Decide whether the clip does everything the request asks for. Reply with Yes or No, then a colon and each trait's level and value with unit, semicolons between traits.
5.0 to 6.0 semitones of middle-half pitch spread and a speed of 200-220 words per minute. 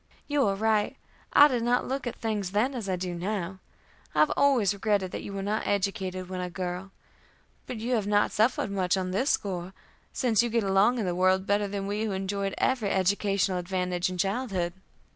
No: average, 2.9 semitones; fast, 205 wpm